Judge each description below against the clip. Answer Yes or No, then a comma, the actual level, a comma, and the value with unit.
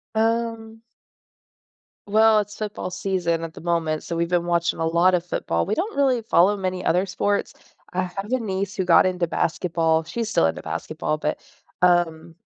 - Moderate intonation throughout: Yes, average, 3.9 semitones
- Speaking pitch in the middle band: Yes, medium, 180 Hz